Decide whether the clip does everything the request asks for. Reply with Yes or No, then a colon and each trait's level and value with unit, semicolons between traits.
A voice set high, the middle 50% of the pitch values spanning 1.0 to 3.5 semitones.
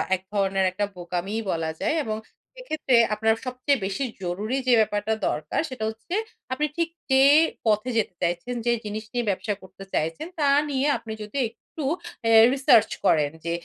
No: high, 220 Hz; average, 4.9 semitones